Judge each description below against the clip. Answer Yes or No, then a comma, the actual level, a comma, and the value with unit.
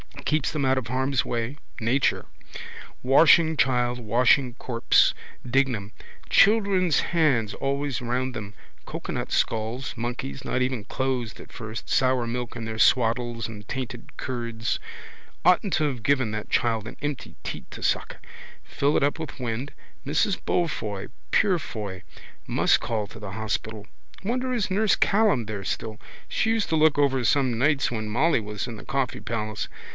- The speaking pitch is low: Yes, low, 125 Hz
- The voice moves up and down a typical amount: Yes, average, 4.3 semitones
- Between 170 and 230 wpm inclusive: No, average, 155 wpm